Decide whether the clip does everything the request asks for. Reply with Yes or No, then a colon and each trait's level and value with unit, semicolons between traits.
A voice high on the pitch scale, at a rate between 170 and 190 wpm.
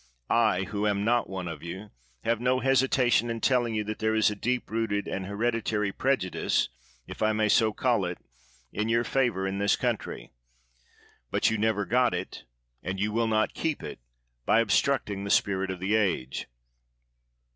No: low, 110 Hz; average, 180 wpm